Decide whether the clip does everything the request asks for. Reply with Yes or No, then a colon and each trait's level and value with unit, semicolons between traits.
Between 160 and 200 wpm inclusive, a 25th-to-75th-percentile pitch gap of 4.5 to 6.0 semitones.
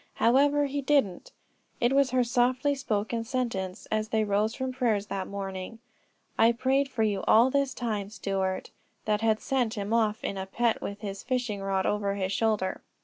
No: average, 180 wpm; average, 4.0 semitones